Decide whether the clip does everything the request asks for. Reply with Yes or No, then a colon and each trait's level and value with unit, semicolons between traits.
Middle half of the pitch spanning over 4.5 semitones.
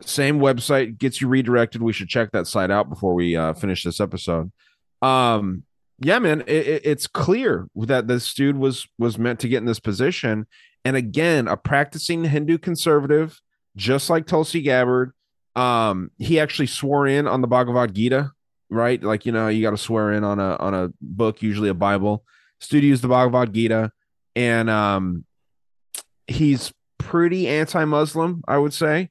Yes: average, 5.1 semitones